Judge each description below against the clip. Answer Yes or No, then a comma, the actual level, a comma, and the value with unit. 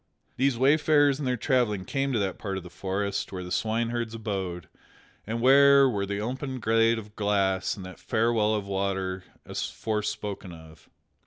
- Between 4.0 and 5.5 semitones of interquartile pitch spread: Yes, average, 4.3 semitones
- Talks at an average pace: Yes, average, 170 wpm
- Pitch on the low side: Yes, low, 105 Hz